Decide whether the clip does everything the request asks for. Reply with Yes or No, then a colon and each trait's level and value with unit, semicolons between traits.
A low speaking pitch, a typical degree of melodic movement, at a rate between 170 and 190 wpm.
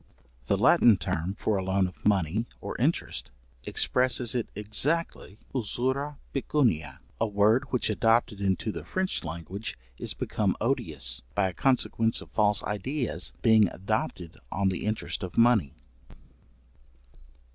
No: low, 105 Hz; average, 4.4 semitones; slow, 135 wpm